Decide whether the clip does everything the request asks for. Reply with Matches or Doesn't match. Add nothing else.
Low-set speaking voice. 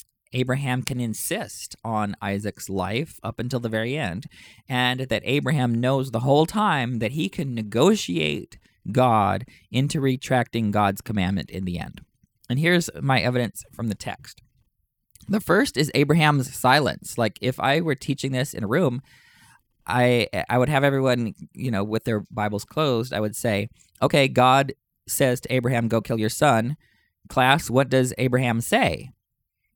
Matches